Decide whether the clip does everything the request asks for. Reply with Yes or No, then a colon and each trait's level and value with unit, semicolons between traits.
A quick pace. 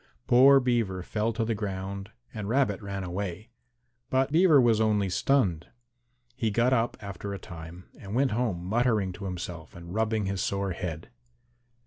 No: average, 160 wpm